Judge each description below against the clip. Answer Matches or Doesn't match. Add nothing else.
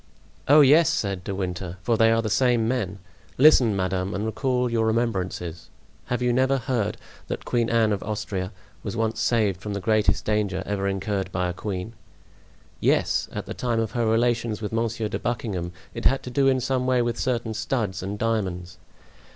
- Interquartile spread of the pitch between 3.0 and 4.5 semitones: Matches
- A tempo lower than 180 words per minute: Doesn't match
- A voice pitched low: Matches